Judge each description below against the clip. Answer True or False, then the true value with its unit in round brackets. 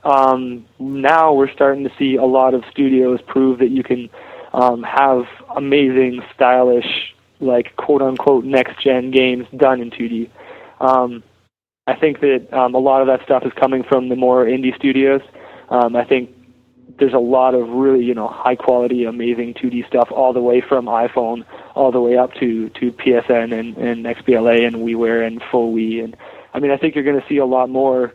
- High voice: False (125 Hz)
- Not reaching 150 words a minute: False (190 wpm)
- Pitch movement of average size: False (1.8 semitones)